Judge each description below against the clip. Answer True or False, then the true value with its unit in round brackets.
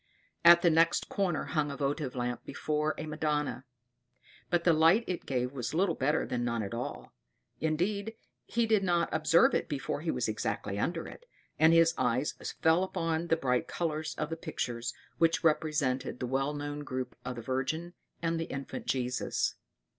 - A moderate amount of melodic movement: True (4.4 semitones)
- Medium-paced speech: True (175 wpm)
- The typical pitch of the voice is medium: True (155 Hz)